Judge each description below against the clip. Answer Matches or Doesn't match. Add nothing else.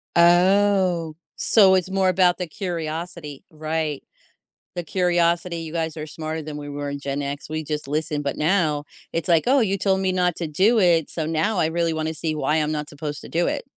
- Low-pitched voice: Doesn't match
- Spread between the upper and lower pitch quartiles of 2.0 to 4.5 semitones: Matches